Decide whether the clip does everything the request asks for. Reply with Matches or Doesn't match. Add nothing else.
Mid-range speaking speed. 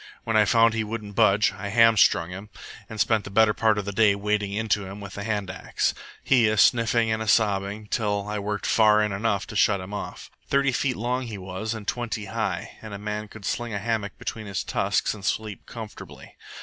Doesn't match